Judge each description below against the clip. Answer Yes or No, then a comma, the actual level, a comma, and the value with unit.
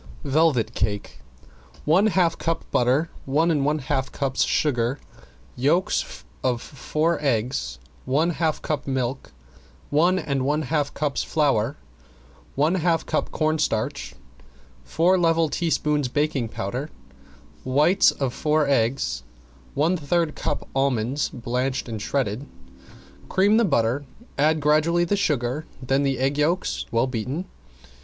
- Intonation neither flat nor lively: Yes, average, 3.7 semitones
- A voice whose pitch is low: No, medium, 145 Hz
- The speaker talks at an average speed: No, slow, 120 wpm